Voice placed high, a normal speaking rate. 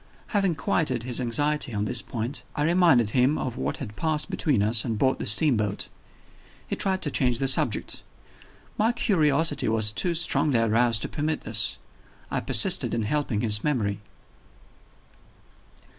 No: low, 130 Hz; average, 155 wpm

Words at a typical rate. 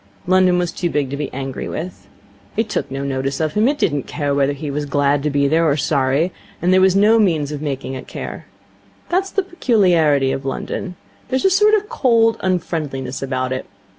No: fast, 220 wpm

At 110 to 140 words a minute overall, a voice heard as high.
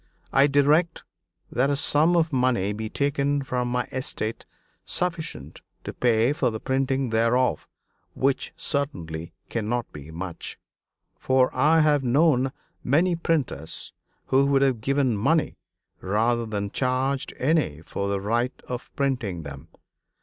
No: slow, 135 wpm; low, 130 Hz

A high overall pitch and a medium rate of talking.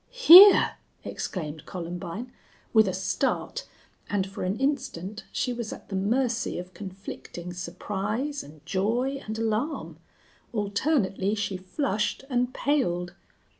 No: high, 210 Hz; slow, 120 wpm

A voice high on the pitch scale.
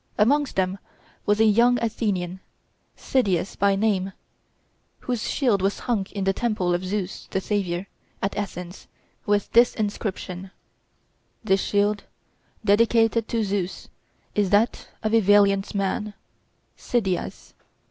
Yes: high, 205 Hz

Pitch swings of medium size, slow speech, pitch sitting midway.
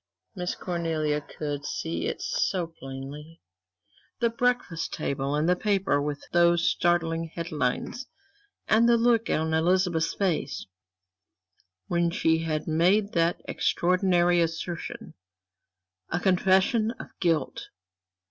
Yes: average, 3.1 semitones; slow, 110 wpm; medium, 170 Hz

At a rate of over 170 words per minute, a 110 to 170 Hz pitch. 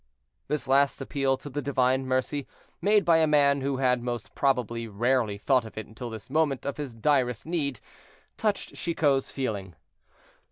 No: average, 165 wpm; low, 135 Hz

